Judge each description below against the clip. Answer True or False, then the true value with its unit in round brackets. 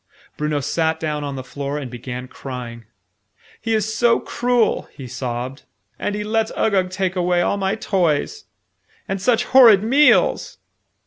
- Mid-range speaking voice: True (180 Hz)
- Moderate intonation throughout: False (7.9 semitones)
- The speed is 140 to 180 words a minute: True (150 wpm)